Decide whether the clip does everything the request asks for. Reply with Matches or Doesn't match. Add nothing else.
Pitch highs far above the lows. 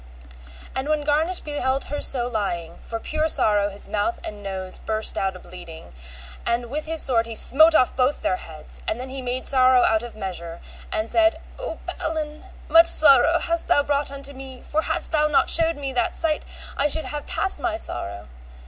Matches